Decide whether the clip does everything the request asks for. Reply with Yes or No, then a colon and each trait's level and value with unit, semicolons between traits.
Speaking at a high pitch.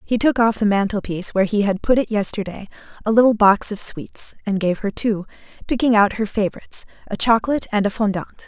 Yes: high, 210 Hz